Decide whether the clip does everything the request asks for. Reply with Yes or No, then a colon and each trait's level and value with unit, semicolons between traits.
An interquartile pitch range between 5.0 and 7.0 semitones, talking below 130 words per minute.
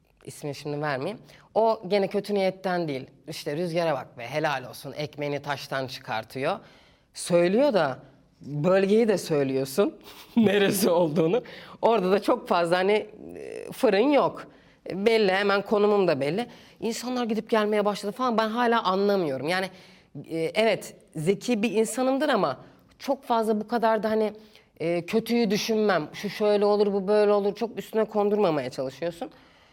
No: wide, 5.5 semitones; average, 135 wpm